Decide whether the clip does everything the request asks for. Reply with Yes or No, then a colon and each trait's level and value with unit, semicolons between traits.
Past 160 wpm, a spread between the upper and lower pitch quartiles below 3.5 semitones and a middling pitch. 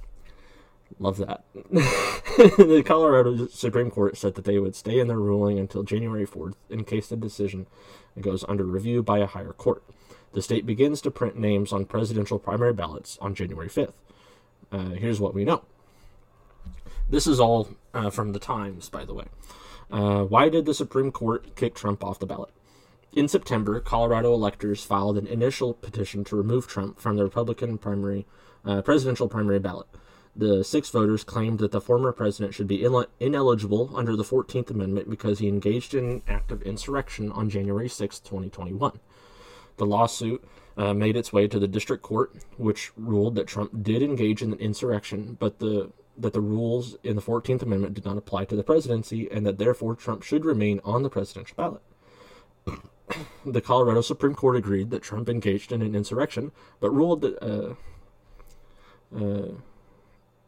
No: average, 170 wpm; average, 2.9 semitones; low, 100 Hz